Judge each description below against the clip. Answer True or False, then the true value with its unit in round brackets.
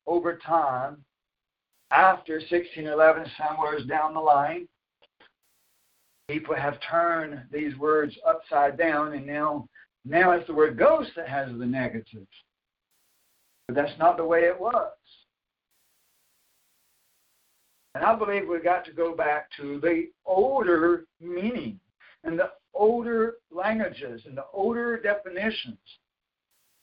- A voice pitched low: False (165 Hz)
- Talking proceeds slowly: True (120 wpm)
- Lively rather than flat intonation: False (4.1 semitones)